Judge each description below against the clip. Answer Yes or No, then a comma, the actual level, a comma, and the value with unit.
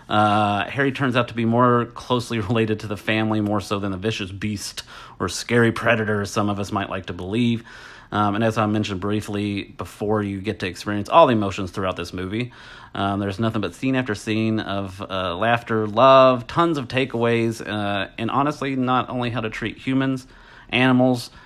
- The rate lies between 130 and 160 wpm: No, average, 195 wpm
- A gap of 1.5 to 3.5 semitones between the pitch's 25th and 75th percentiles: Yes, average, 2.9 semitones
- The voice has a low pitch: Yes, low, 110 Hz